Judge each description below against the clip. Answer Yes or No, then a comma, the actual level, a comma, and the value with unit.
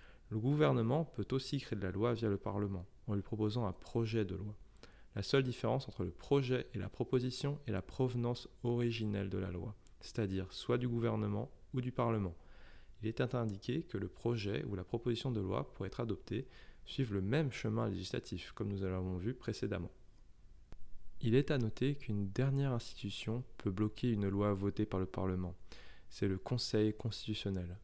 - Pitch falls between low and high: No, low, 110 Hz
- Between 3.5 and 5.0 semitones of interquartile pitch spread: Yes, average, 3.9 semitones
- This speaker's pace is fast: No, average, 180 wpm